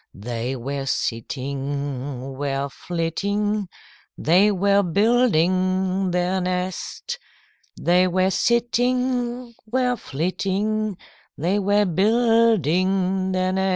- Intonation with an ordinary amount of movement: Yes, average, 4.9 semitones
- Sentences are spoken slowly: Yes, slow, 85 wpm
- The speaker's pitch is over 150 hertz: Yes, medium, 185 Hz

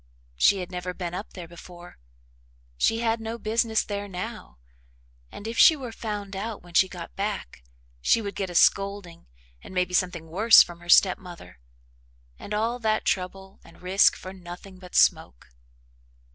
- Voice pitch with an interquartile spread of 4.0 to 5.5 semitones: No, average, 3.2 semitones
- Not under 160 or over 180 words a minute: Yes, average, 170 wpm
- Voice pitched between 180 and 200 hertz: Yes, high, 190 Hz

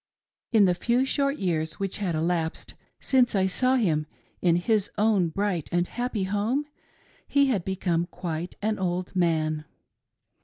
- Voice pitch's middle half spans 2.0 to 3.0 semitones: No, average, 4.4 semitones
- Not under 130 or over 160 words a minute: Yes, average, 150 wpm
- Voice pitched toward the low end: No, high, 190 Hz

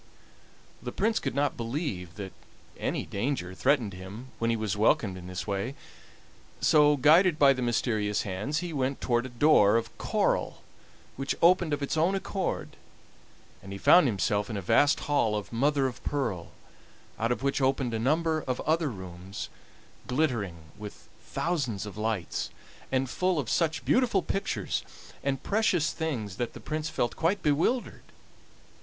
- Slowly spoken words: No, average, 160 wpm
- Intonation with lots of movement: Yes, wide, 6.6 semitones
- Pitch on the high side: No, low, 130 Hz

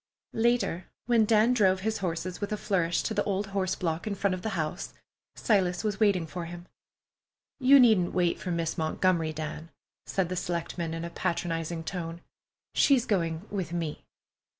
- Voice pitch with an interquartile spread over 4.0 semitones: No, average, 3.5 semitones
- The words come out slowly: No, average, 175 wpm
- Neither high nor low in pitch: Yes, medium, 180 Hz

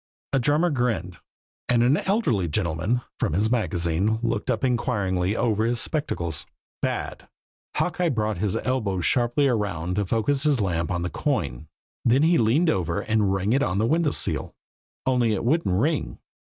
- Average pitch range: No, wide, 5.9 semitones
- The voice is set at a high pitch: No, low, 110 Hz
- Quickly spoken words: No, average, 165 wpm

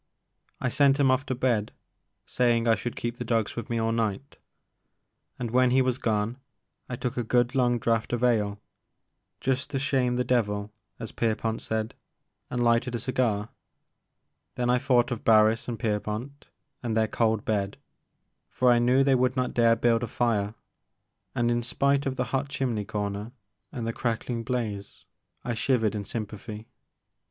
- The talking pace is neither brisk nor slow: Yes, average, 175 wpm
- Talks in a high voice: No, low, 120 Hz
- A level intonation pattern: Yes, narrow, 2.3 semitones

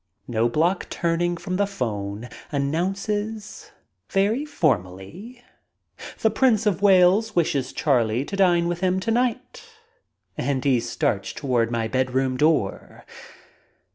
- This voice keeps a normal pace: No, slow, 130 wpm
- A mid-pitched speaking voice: Yes, medium, 170 Hz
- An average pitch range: No, wide, 7.8 semitones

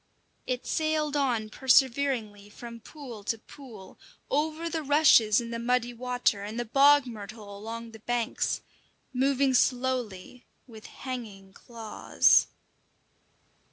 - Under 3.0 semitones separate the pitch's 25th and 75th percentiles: No, average, 3.7 semitones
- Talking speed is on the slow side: Yes, slow, 120 wpm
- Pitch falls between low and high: No, high, 240 Hz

